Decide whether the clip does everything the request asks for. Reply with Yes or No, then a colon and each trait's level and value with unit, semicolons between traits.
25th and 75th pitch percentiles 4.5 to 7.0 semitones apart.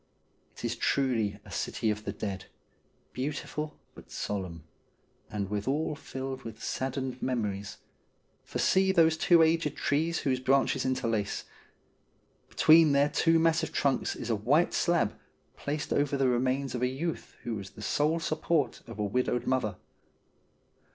Yes: wide, 5.5 semitones